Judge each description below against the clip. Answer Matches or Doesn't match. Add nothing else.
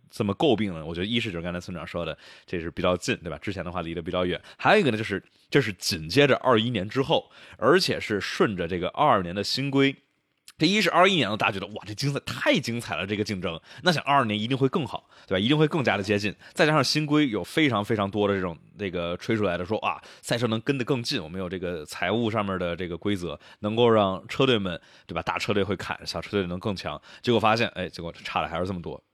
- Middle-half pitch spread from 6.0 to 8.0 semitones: Doesn't match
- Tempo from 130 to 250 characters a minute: Doesn't match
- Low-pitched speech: Matches